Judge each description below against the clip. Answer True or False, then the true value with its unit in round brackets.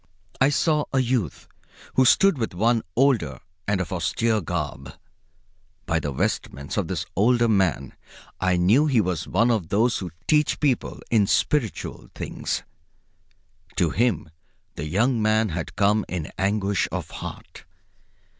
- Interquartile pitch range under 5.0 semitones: False (5.5 semitones)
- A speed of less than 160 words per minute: True (140 wpm)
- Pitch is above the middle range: False (105 Hz)